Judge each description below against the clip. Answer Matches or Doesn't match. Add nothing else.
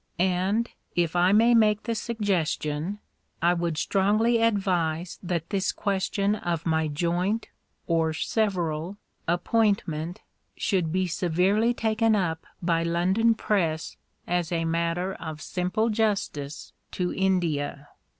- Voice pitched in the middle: Matches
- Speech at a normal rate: Doesn't match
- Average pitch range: Matches